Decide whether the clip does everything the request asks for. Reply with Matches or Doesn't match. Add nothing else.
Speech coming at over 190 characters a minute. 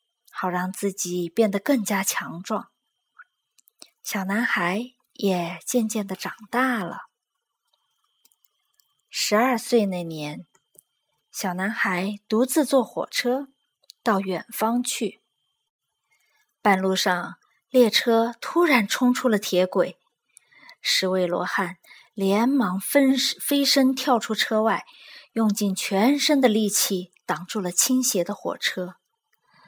Doesn't match